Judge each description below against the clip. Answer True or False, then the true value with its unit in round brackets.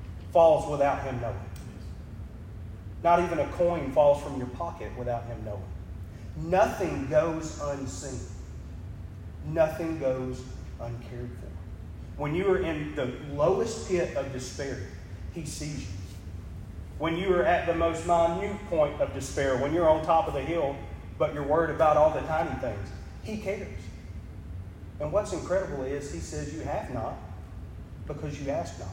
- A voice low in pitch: True (120 Hz)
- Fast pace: False (155 wpm)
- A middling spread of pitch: False (8.6 semitones)